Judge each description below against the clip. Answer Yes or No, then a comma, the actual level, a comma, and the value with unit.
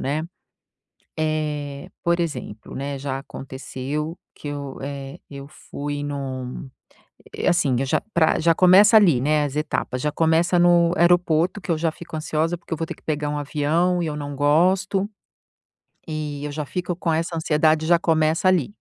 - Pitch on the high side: No, medium, 155 Hz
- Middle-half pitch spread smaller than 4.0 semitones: Yes, average, 2.9 semitones